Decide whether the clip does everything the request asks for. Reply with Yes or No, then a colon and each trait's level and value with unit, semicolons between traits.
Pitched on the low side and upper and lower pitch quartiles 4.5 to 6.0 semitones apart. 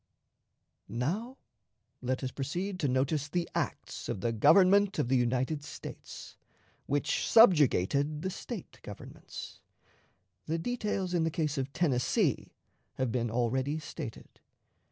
No: medium, 150 Hz; wide, 5.5 semitones